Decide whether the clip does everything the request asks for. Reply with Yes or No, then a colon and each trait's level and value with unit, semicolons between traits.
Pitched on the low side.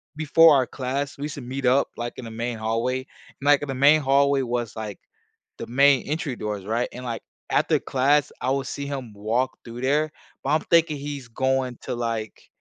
Yes: low, 130 Hz